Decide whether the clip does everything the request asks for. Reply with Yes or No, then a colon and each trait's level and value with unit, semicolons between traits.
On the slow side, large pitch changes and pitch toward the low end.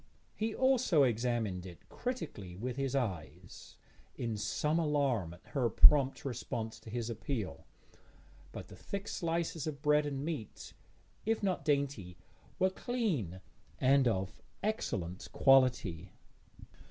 Yes: slow, 125 wpm; wide, 6.5 semitones; low, 130 Hz